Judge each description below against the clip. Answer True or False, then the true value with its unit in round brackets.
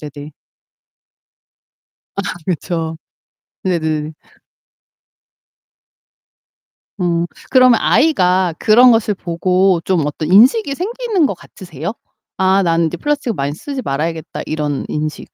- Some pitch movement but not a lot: False (6.6 semitones)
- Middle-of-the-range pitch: True (180 Hz)